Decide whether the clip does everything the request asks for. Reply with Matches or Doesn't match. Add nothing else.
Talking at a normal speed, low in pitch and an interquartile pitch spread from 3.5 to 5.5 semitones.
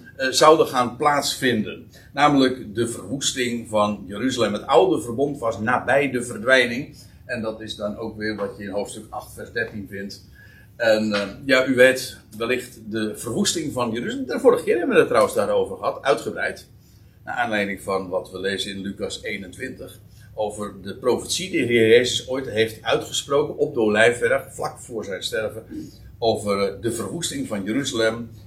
Matches